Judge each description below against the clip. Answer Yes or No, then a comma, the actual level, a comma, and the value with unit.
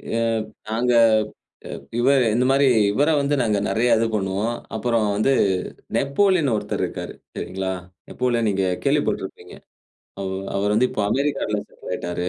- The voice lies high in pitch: No, low, 115 Hz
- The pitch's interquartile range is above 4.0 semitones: Yes, average, 4.7 semitones